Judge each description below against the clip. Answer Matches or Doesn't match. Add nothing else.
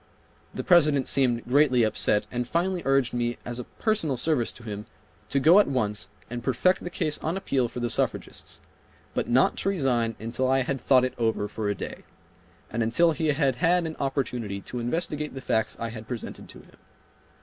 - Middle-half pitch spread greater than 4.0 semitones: Matches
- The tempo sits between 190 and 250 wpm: Matches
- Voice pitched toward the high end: Doesn't match